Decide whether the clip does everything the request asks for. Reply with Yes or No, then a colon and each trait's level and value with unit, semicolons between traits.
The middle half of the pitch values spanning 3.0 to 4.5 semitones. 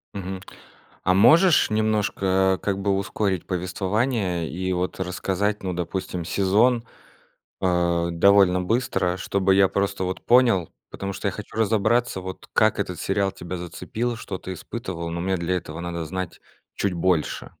No: narrow, 2.4 semitones